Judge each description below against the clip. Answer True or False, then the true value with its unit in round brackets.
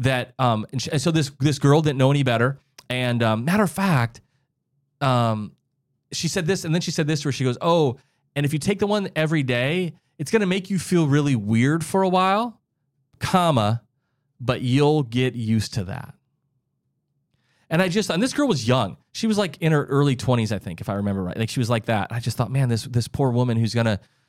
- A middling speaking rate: False (225 wpm)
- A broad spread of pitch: False (4.4 semitones)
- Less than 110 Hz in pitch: False (140 Hz)